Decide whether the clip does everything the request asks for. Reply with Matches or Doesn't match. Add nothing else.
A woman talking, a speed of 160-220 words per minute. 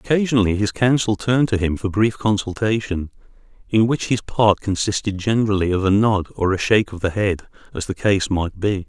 Doesn't match